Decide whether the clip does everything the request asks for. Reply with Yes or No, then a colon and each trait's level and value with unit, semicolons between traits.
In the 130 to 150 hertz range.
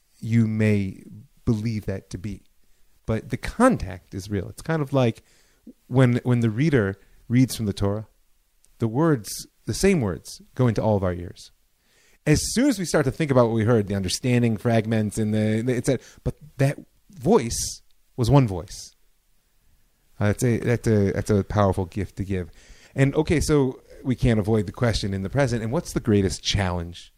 No: low, 110 Hz